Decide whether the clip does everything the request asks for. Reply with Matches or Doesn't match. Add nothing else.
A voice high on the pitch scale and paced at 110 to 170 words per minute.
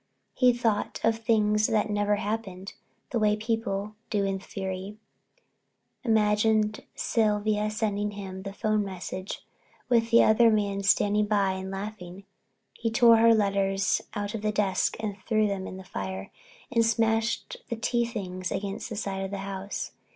Matches